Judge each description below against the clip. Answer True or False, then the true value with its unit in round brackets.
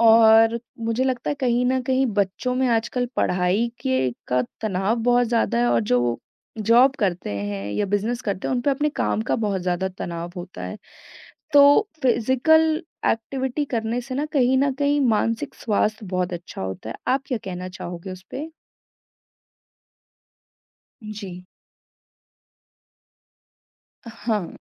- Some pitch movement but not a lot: False (5.9 semitones)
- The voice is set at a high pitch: True (225 Hz)